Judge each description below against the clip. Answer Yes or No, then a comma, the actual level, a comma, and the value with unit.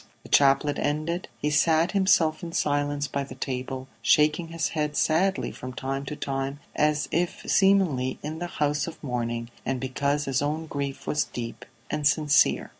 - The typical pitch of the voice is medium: Yes, medium, 145 Hz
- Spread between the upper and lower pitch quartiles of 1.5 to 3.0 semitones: Yes, narrow, 2.6 semitones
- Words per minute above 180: No, average, 170 wpm